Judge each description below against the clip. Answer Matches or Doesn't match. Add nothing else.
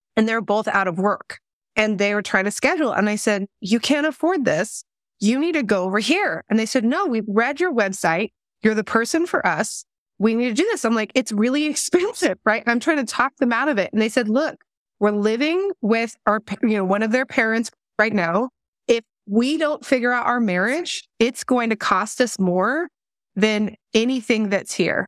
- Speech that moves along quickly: Matches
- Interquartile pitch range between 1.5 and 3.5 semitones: Doesn't match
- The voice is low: Doesn't match